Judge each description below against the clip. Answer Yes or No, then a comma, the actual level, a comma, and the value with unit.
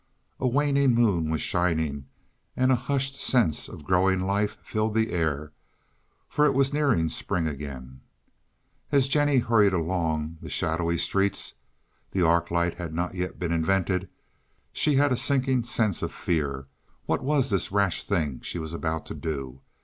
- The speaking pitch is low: Yes, very low, 90 Hz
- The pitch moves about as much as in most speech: No, wide, 7.4 semitones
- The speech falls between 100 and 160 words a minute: Yes, average, 155 wpm